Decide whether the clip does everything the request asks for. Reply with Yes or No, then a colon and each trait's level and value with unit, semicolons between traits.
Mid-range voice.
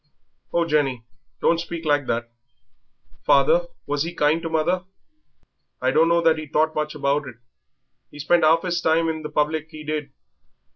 Yes: medium, 155 Hz